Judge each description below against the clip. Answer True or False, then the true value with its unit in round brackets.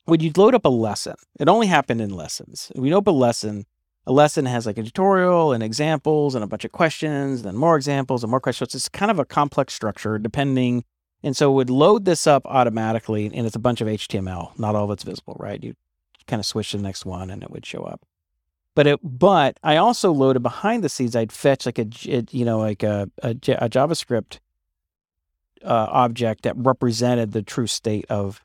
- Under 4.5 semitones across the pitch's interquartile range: False (5.2 semitones)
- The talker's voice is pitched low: True (120 Hz)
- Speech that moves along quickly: True (220 wpm)